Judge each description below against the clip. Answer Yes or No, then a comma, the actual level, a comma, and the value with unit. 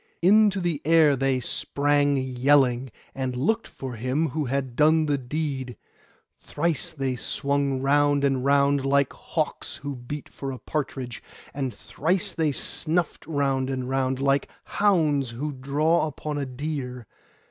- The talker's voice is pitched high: No, medium, 140 Hz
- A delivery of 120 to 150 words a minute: Yes, average, 145 wpm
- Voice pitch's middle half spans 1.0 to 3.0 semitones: Yes, narrow, 2.6 semitones